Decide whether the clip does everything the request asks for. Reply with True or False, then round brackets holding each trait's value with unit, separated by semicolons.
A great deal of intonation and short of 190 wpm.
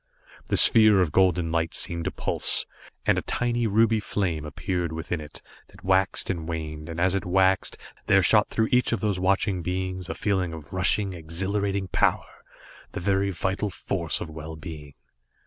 False (3.2 semitones; 175 wpm)